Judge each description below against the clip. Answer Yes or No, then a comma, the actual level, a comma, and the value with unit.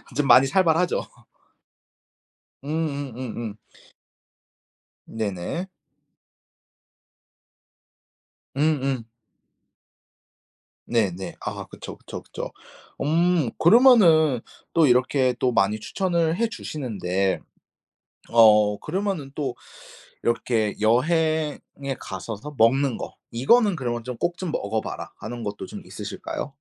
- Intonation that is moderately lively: No, wide, 6.1 semitones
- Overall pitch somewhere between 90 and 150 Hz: Yes, low, 135 Hz